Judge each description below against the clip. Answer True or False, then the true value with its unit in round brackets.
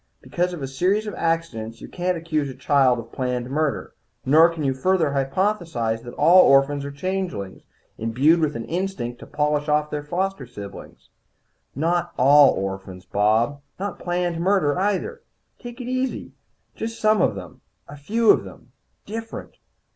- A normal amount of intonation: False (5.9 semitones)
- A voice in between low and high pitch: True (150 Hz)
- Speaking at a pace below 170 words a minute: True (160 wpm)